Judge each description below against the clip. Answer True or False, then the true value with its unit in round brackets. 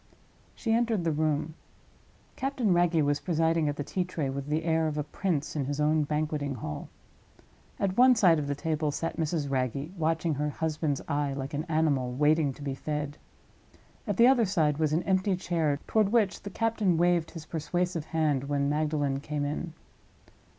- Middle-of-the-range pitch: True (155 Hz)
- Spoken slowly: False (185 wpm)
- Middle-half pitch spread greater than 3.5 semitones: False (3.2 semitones)